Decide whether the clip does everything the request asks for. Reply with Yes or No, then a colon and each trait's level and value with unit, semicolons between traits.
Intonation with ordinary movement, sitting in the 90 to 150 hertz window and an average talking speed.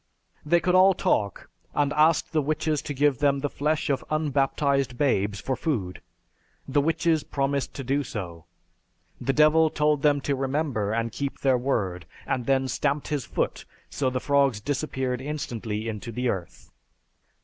Yes: average, 3.3 semitones; medium, 140 Hz; average, 160 wpm